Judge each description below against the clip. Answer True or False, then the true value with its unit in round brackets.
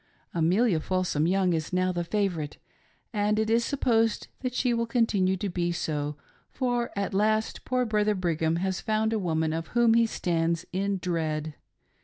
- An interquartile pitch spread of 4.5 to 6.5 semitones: True (4.9 semitones)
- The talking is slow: False (180 wpm)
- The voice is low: False (190 Hz)